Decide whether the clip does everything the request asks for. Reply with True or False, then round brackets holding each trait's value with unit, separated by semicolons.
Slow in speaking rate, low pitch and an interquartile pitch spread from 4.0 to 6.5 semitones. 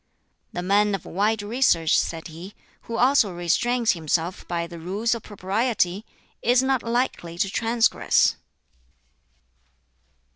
False (120 wpm; 205 Hz; 5.0 semitones)